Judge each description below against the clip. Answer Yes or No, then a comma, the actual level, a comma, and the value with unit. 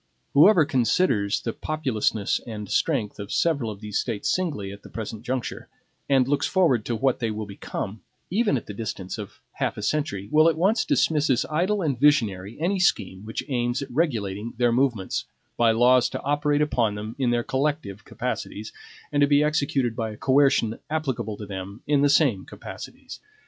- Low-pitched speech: Yes, low, 125 Hz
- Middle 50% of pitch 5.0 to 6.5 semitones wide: Yes, wide, 5.5 semitones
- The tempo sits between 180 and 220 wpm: Yes, average, 185 wpm